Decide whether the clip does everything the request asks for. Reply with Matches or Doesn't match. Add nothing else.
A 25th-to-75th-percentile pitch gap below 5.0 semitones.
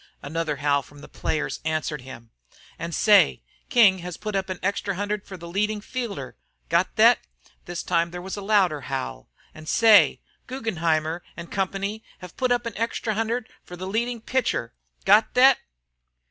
Doesn't match